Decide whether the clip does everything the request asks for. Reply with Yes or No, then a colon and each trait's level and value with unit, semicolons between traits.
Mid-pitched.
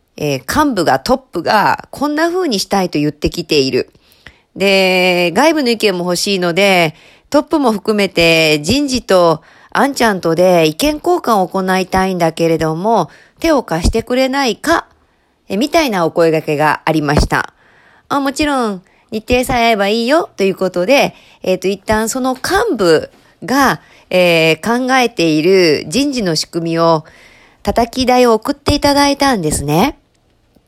No: high, 200 Hz